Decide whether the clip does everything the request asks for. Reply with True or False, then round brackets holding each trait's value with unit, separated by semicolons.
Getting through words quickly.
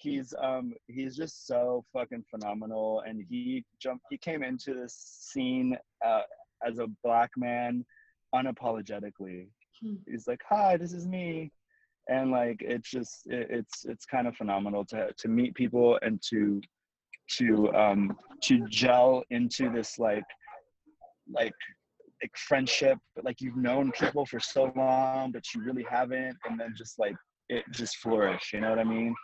False (155 wpm)